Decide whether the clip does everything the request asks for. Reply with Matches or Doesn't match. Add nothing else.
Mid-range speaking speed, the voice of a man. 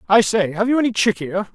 Doesn't match